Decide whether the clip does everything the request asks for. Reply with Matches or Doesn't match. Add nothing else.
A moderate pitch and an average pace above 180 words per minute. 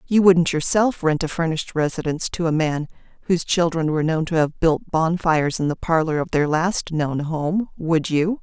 Matches